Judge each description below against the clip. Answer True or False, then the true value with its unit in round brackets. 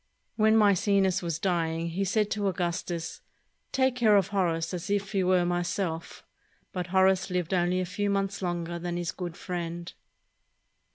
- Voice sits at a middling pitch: True (180 Hz)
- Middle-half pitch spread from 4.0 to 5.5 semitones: False (2.4 semitones)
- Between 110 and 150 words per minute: False (160 wpm)